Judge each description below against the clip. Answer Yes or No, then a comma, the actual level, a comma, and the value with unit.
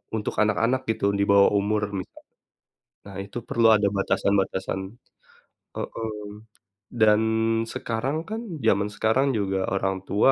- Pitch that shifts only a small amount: Yes, narrow, 2.2 semitones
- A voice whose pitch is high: No, low, 105 Hz